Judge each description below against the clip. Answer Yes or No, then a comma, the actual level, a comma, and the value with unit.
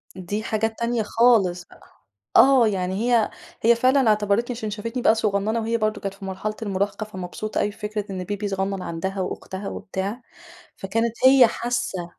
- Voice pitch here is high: Yes, high, 210 Hz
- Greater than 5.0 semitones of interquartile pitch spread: No, average, 3.1 semitones